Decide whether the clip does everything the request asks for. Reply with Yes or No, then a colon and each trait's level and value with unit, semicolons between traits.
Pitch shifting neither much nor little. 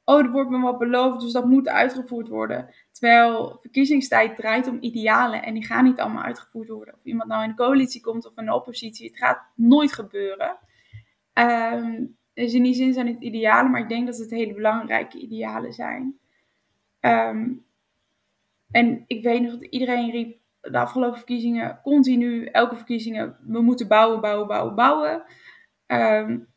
No: narrow, 2.1 semitones